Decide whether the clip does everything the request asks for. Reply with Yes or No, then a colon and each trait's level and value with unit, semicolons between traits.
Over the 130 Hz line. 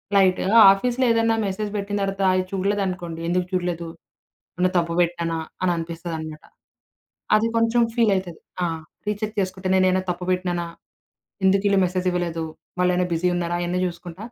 Yes: medium, 185 Hz